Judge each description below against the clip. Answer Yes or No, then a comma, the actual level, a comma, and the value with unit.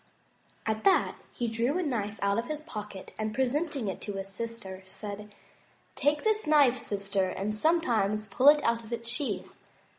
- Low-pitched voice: No, high, 230 Hz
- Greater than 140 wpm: Yes, average, 175 wpm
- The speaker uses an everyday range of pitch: No, wide, 5.8 semitones